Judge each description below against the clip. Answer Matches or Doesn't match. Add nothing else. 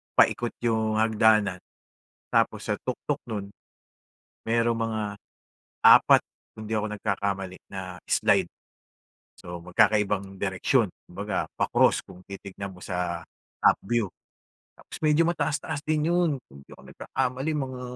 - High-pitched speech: Doesn't match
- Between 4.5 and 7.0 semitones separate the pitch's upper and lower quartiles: Doesn't match